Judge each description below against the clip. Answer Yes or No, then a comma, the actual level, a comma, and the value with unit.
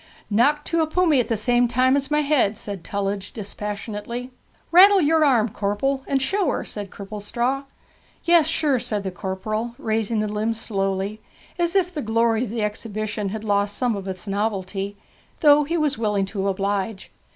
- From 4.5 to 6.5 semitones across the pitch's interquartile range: Yes, average, 5.2 semitones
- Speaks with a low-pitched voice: No, high, 220 Hz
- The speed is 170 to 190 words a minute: Yes, average, 175 wpm